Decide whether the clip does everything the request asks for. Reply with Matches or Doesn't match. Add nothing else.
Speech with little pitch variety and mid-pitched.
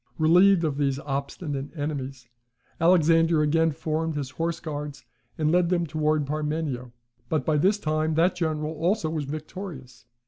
Matches